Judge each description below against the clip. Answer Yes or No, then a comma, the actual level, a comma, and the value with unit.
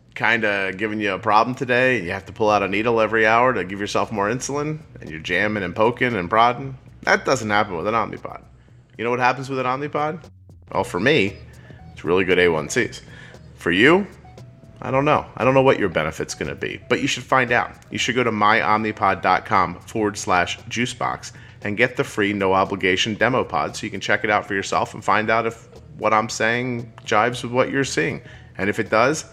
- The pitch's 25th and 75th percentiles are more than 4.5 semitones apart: No, average, 3.3 semitones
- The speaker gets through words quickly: Yes, fast, 215 wpm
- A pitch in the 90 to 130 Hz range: Yes, low, 115 Hz